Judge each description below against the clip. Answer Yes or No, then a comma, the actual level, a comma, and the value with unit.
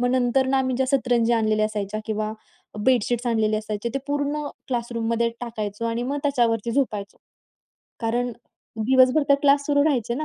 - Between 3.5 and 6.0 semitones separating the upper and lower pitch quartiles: No, average, 3.1 semitones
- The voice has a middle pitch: No, high, 240 Hz